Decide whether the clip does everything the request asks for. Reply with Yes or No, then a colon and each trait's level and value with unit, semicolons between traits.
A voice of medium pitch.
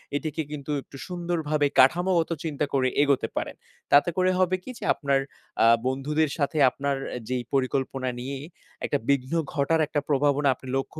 Yes: medium, 145 Hz